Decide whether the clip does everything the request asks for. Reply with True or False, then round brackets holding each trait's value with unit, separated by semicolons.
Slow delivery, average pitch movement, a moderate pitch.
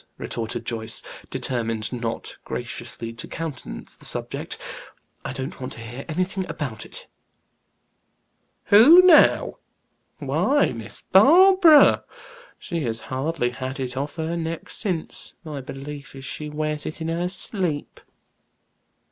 False (125 wpm; 6.0 semitones; 150 Hz)